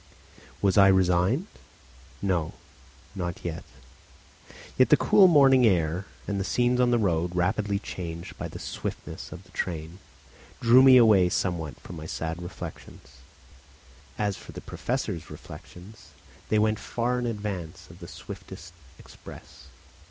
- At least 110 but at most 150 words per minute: Yes, average, 140 wpm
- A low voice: Yes, very low, 95 Hz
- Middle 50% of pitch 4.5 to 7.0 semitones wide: Yes, average, 5.1 semitones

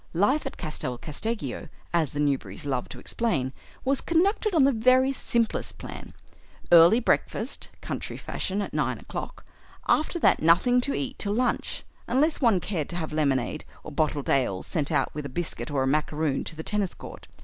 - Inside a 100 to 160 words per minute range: No, average, 180 wpm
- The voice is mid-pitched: Yes, medium, 175 Hz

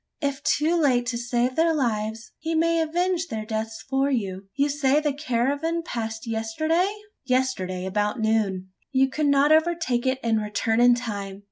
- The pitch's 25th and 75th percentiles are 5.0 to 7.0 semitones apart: Yes, average, 5.3 semitones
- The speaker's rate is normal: Yes, average, 165 wpm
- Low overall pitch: No, very high, 255 Hz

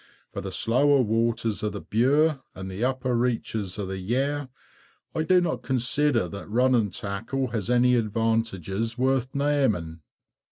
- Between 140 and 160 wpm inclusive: Yes, average, 150 wpm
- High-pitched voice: No, low, 120 Hz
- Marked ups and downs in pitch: No, average, 4.0 semitones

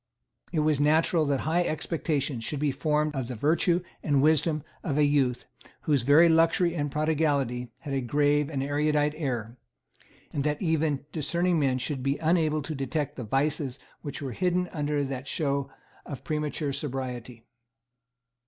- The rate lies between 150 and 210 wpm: Yes, average, 160 wpm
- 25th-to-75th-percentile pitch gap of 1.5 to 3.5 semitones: Yes, narrow, 2.4 semitones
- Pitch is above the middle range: No, medium, 145 Hz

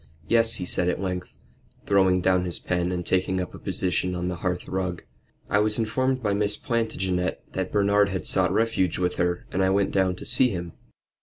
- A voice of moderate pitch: No, very low, 95 Hz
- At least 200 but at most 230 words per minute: Yes, fast, 205 wpm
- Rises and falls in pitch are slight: Yes, narrow, 2.3 semitones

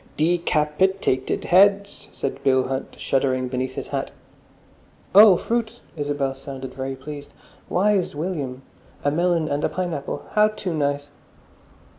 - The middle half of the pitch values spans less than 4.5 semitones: No, wide, 5.4 semitones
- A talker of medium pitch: Yes, medium, 145 Hz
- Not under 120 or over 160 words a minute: Yes, average, 140 wpm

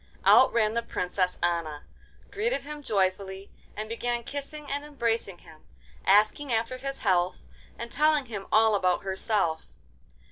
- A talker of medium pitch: No, high, 220 Hz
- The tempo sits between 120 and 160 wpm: Yes, average, 140 wpm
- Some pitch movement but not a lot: No, wide, 6.2 semitones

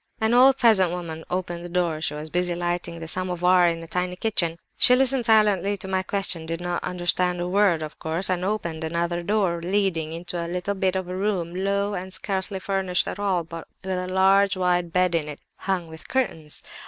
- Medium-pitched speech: Yes, medium, 180 Hz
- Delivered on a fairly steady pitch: Yes, narrow, 2.3 semitones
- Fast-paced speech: Yes, fast, 210 wpm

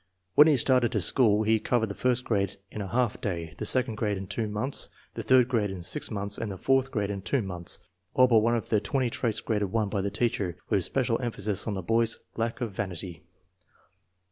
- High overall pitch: No, low, 110 Hz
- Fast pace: Yes, fast, 225 wpm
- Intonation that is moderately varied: Yes, average, 3.3 semitones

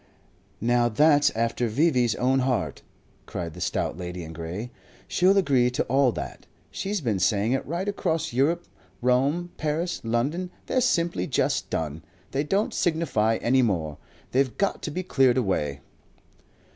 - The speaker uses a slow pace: No, average, 150 wpm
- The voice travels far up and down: Yes, wide, 6.7 semitones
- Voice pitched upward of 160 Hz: No, low, 130 Hz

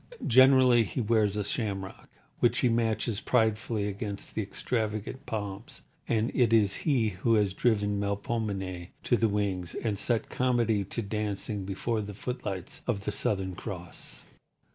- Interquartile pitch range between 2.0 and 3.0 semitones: Yes, narrow, 2.6 semitones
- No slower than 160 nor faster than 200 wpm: No, average, 145 wpm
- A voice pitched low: Yes, low, 105 Hz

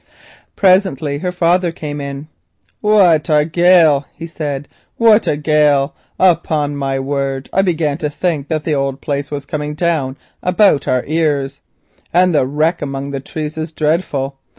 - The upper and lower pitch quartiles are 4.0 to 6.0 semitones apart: No, average, 3.2 semitones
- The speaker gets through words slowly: No, average, 155 wpm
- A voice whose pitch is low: No, medium, 150 Hz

